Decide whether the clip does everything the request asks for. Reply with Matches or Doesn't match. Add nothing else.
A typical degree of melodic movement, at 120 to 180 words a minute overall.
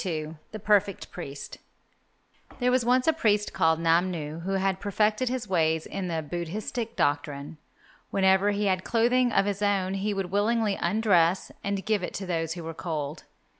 Matches